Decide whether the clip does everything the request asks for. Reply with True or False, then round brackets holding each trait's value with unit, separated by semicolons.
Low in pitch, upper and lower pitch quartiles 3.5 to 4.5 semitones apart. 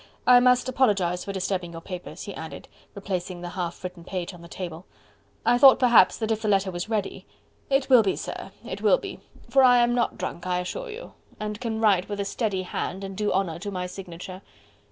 False (195 Hz; 4.2 semitones)